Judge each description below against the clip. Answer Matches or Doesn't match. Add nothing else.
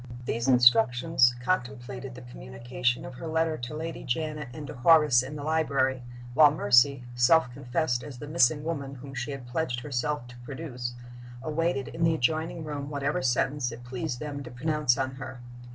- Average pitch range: Matches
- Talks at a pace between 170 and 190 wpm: Matches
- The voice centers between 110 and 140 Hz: Matches